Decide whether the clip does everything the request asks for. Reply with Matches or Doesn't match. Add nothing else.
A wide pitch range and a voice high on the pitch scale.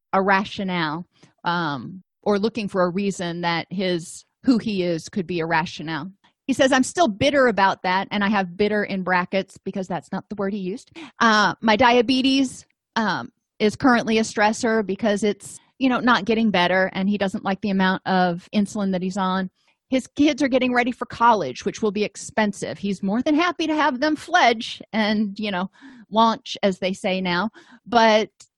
Doesn't match